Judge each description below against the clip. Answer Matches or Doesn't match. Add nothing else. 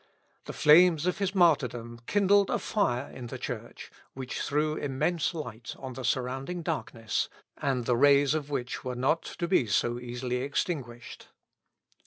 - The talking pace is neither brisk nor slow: Matches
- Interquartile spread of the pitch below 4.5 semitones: Doesn't match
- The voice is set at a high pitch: Doesn't match